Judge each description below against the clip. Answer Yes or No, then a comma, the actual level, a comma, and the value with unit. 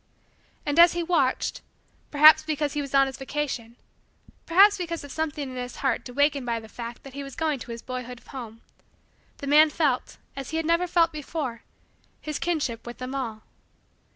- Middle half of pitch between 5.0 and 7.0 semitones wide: No, average, 3.9 semitones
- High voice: Yes, very high, 280 Hz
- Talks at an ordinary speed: Yes, average, 185 wpm